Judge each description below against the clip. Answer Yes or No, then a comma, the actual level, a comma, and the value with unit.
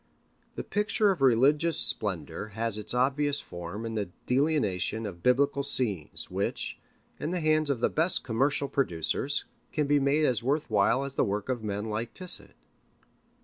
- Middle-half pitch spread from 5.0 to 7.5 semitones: Yes, average, 5.3 semitones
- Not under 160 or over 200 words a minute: Yes, average, 165 wpm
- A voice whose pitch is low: Yes, low, 130 Hz